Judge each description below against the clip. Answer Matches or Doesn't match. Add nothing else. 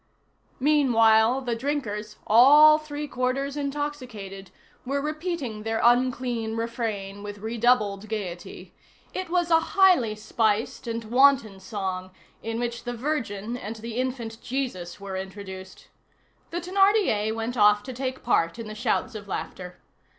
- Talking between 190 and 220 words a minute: Doesn't match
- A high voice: Matches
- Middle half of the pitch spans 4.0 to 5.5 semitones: Matches